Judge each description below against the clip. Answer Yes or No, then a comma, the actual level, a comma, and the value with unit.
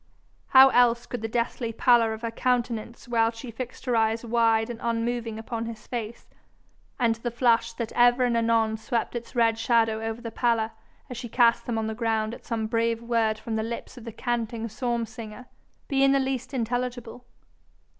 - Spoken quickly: No, average, 195 wpm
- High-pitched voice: Yes, high, 230 Hz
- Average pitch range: No, narrow, 1.2 semitones